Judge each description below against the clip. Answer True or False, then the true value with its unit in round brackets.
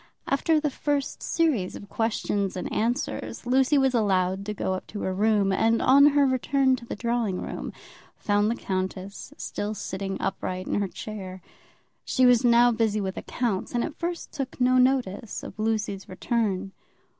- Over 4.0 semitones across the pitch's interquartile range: True (4.7 semitones)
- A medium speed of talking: True (170 wpm)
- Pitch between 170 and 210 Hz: False (220 Hz)